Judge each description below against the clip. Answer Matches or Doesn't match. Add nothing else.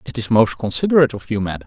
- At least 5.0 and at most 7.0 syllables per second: Doesn't match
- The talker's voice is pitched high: Doesn't match